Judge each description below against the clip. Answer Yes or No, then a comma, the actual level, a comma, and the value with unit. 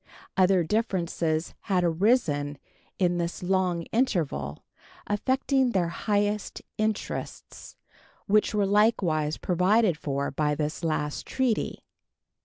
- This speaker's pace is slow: Yes, slow, 100 wpm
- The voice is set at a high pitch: No, medium, 180 Hz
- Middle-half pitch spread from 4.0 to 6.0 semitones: Yes, average, 5.0 semitones